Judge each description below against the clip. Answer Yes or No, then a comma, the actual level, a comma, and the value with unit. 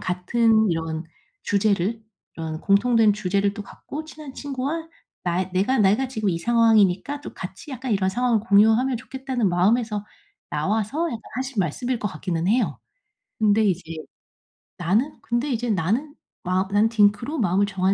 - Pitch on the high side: Yes, high, 215 Hz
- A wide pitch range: No, average, 4.6 semitones